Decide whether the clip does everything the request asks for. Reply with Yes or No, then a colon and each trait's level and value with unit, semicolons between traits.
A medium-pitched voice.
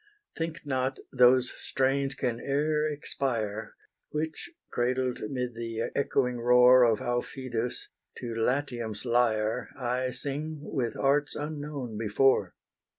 No: low, 125 Hz